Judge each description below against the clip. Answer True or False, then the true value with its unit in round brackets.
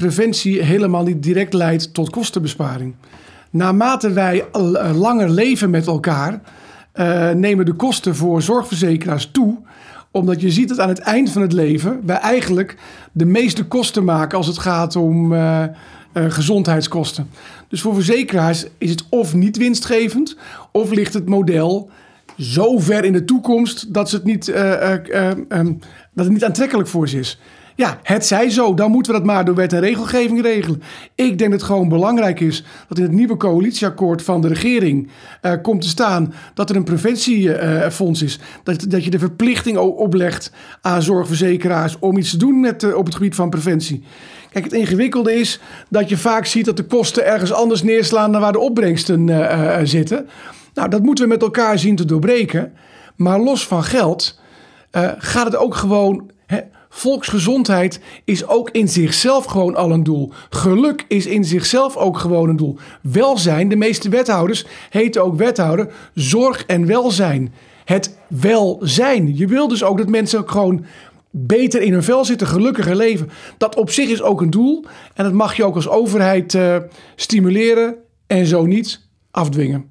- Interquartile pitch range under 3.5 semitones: False (4.5 semitones)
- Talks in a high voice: True (195 Hz)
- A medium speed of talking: True (175 wpm)